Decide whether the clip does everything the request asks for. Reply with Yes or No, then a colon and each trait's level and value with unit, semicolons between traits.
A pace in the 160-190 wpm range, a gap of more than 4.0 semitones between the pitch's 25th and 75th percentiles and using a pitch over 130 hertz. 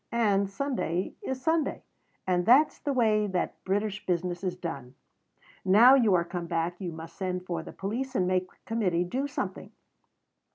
Yes: average, 170 wpm; average, 4.6 semitones; high, 190 Hz